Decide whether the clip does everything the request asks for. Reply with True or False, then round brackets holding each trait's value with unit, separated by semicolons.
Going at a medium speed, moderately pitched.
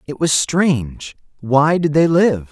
True (145 wpm; 150 Hz)